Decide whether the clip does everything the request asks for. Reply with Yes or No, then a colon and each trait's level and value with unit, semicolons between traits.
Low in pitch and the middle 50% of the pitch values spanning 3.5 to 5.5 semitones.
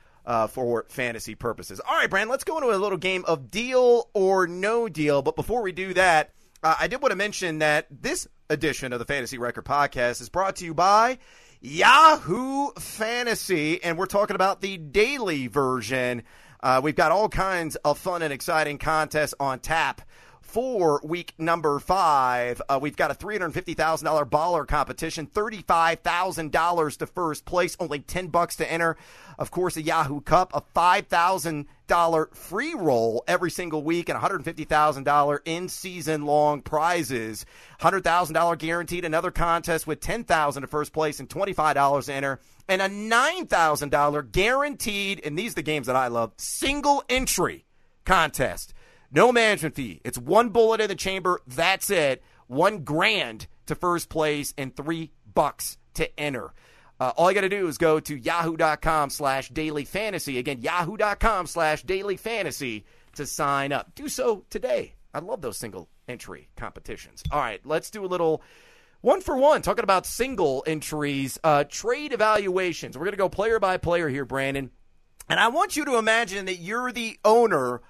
No: medium, 165 Hz; average, 4.9 semitones